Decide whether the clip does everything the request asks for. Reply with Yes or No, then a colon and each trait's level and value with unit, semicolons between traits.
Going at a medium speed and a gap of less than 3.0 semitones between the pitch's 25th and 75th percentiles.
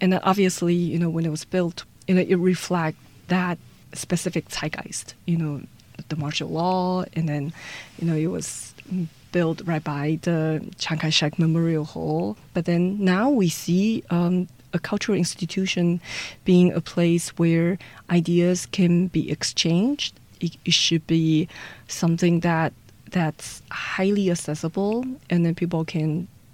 Yes: average, 145 wpm; narrow, 2.5 semitones